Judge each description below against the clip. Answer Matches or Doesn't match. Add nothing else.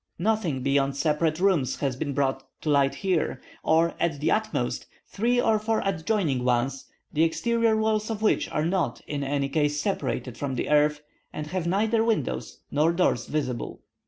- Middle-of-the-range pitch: Matches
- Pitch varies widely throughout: Matches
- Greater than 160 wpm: Matches